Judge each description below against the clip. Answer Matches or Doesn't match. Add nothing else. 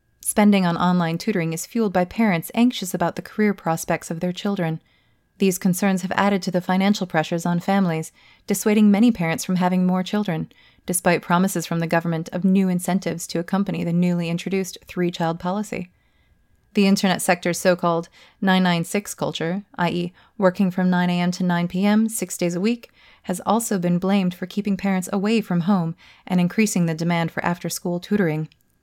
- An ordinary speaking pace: Matches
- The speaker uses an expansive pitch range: Doesn't match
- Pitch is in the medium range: Matches